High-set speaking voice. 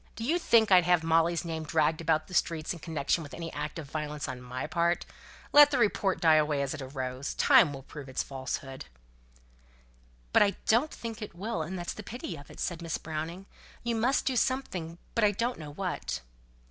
No: medium, 165 Hz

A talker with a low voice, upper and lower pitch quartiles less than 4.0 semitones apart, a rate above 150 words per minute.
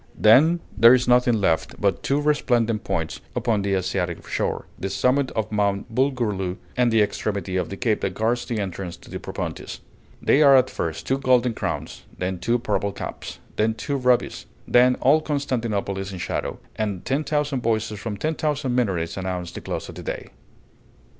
No: low, 110 Hz; average, 4.6 semitones; average, 185 wpm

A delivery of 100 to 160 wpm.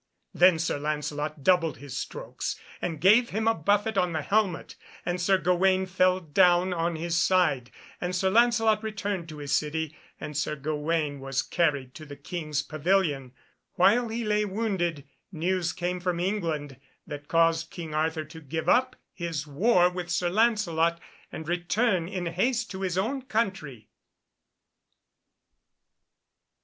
Yes: average, 150 wpm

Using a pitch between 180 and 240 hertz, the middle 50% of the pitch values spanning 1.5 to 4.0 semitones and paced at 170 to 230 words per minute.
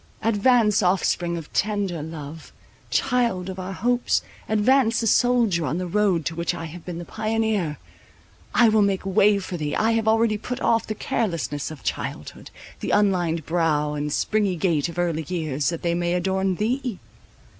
No: high, 190 Hz; average, 4.6 semitones; average, 175 wpm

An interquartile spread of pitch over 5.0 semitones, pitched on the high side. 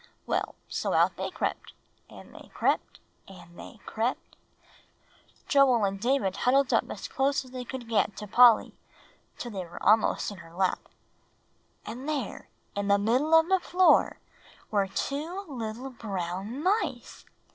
Yes: wide, 5.5 semitones; high, 235 Hz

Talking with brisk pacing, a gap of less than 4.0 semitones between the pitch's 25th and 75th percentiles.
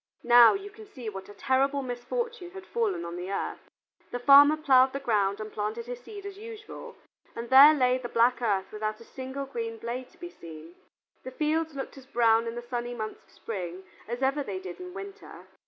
No: fast, 210 wpm; average, 5.1 semitones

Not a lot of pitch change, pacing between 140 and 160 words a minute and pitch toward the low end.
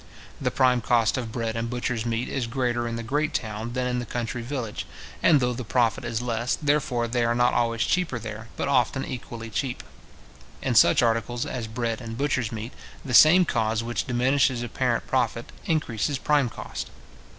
No: narrow, 1.9 semitones; average, 185 wpm; low, 120 Hz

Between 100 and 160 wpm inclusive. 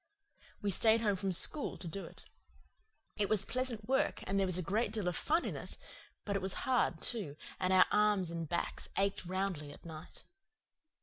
No: average, 195 wpm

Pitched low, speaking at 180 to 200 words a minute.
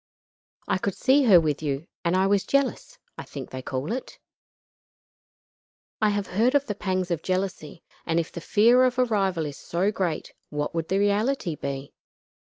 No: high, 190 Hz; average, 185 wpm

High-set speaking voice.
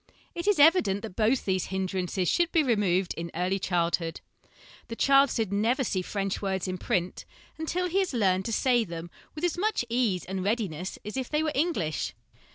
Yes: high, 205 Hz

